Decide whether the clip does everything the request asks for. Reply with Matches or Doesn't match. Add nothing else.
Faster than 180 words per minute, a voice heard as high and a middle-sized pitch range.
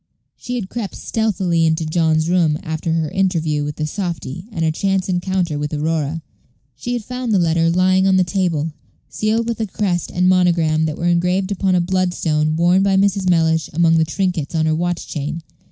Doesn't match